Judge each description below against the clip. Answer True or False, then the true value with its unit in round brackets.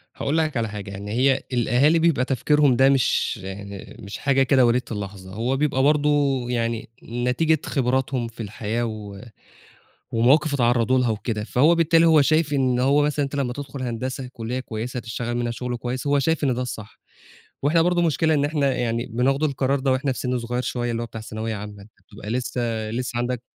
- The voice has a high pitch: False (125 Hz)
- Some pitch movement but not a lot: True (3.3 semitones)